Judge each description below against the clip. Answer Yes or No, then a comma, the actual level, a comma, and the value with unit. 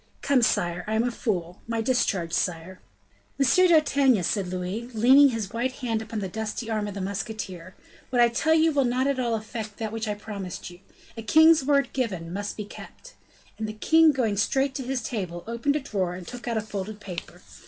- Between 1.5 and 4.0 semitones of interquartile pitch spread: No, average, 4.5 semitones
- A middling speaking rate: No, fast, 210 wpm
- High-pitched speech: Yes, high, 220 Hz